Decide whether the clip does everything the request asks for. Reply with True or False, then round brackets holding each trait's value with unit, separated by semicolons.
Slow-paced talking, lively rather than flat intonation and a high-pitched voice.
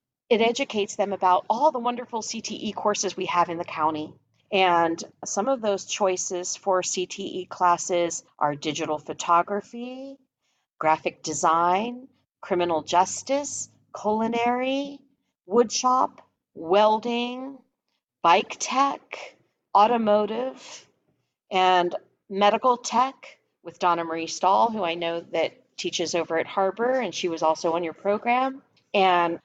True (120 wpm; 5.9 semitones; 195 Hz)